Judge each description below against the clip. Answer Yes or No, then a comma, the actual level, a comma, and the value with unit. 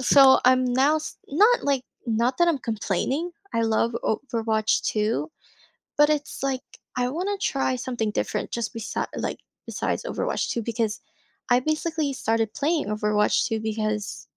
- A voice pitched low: No, very high, 250 Hz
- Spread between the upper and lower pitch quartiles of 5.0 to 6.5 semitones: No, average, 4.5 semitones